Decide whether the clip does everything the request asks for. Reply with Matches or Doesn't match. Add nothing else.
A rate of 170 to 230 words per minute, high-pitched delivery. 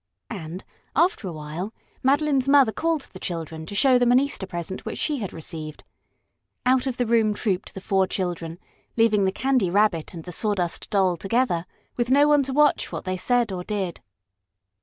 Matches